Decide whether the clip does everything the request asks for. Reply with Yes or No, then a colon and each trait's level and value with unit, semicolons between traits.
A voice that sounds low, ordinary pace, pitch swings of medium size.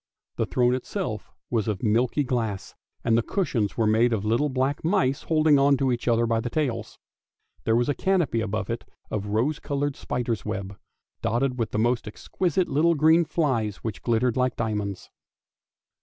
Yes: low, 120 Hz; average, 175 wpm; average, 4.2 semitones